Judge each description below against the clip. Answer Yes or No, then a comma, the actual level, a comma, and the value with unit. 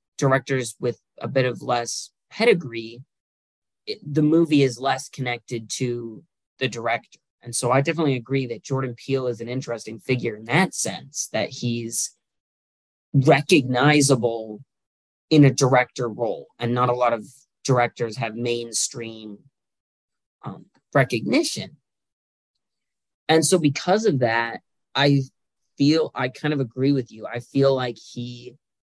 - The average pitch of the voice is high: No, low, 125 Hz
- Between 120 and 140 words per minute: Yes, slow, 135 wpm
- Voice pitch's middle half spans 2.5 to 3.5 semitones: Yes, average, 2.8 semitones